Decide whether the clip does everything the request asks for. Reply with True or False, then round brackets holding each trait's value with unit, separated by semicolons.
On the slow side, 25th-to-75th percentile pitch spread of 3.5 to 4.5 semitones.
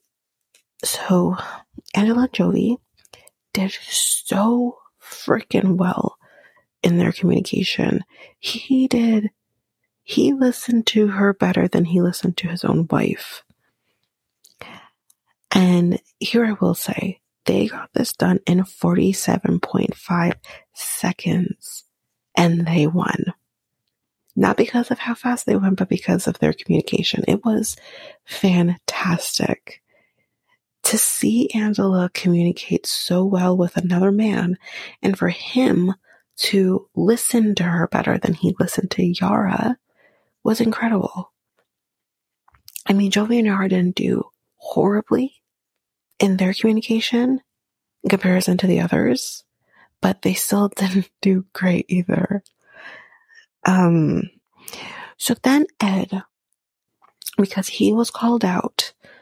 True (110 wpm; 3.9 semitones)